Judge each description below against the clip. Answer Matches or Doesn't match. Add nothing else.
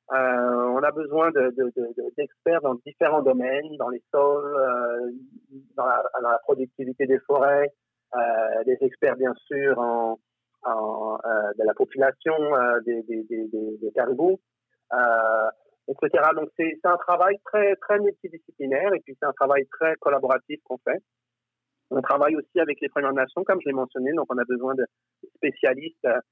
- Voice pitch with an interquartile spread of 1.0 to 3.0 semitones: Doesn't match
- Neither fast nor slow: Matches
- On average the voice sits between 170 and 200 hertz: Doesn't match